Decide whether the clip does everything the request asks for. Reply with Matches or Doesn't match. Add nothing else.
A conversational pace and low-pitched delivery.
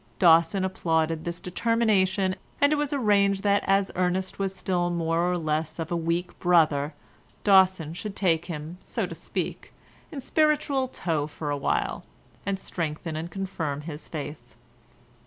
Doesn't match